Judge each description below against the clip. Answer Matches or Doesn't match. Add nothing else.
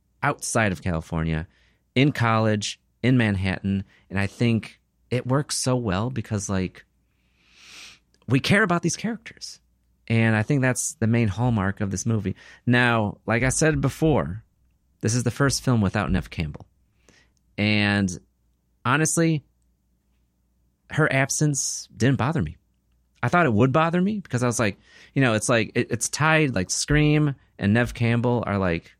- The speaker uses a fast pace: Doesn't match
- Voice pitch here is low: Matches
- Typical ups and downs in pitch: Doesn't match